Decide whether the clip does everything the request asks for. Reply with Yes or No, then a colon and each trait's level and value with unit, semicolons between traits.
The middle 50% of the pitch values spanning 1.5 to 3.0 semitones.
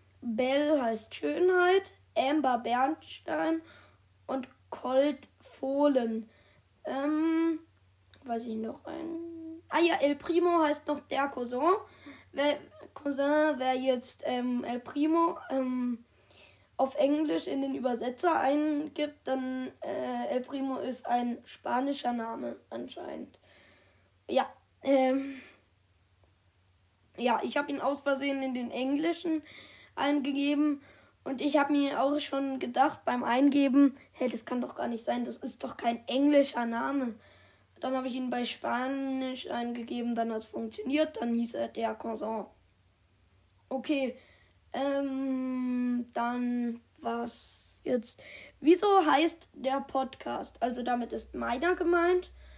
No: average, 3.7 semitones